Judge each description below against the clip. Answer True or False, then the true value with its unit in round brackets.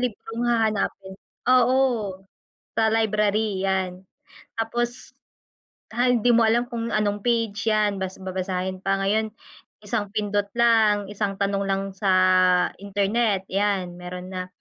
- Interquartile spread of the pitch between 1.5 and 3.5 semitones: True (2.7 semitones)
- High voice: True (205 Hz)